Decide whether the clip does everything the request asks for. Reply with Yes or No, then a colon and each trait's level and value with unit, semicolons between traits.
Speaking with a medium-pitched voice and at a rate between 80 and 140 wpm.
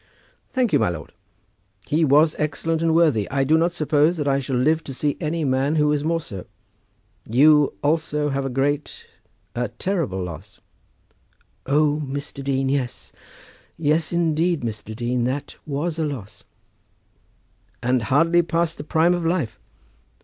No: medium, 145 Hz; average, 155 wpm